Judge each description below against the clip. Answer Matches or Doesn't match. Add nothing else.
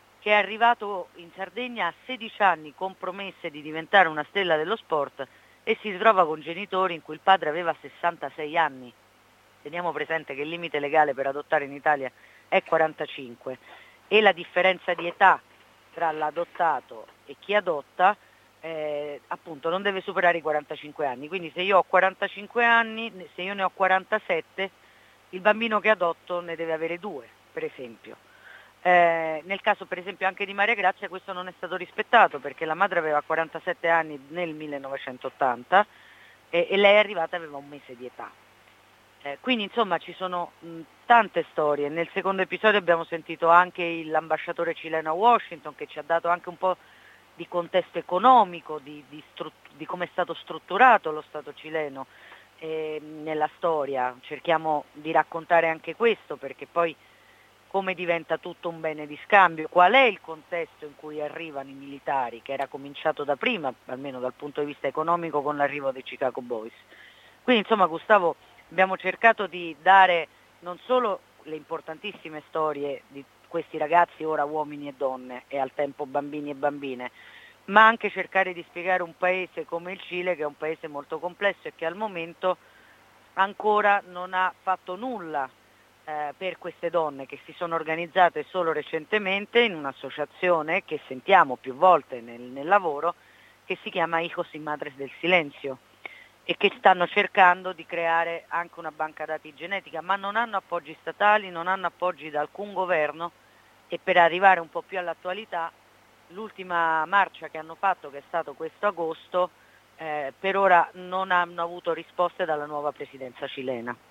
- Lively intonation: Doesn't match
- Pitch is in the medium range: Matches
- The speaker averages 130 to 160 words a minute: Doesn't match